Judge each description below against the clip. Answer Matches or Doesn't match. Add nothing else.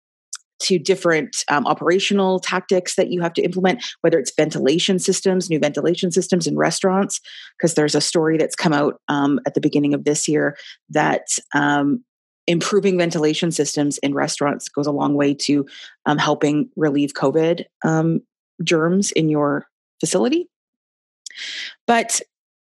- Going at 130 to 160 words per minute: Matches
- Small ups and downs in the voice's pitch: Doesn't match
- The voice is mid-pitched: Matches